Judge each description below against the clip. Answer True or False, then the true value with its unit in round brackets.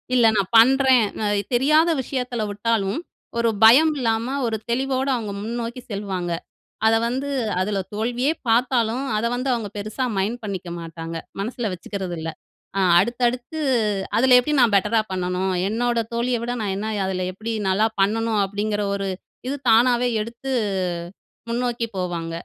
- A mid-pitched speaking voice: False (230 Hz)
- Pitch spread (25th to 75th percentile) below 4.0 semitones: True (3.6 semitones)